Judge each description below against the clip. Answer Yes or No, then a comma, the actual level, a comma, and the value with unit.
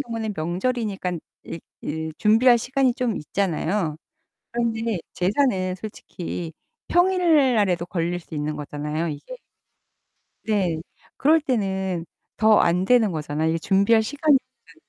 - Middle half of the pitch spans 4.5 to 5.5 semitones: No, wide, 6.0 semitones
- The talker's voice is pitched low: No, high, 200 Hz